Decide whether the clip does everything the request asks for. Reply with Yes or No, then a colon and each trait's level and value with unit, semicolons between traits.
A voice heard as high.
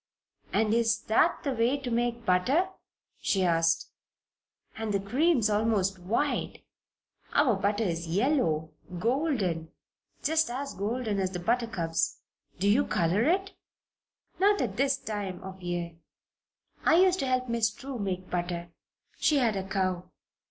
Yes: high, 220 Hz